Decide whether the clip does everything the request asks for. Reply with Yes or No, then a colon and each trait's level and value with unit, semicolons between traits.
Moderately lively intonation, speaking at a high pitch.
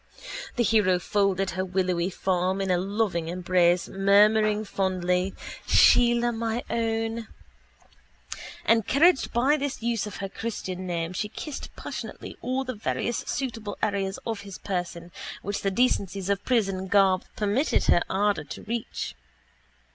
Yes: average, 3.4 semitones; high, 200 Hz